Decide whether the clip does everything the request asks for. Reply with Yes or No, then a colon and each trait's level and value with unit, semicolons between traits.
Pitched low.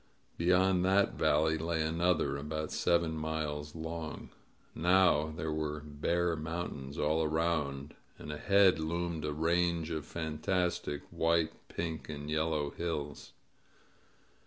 Yes: very low, 80 Hz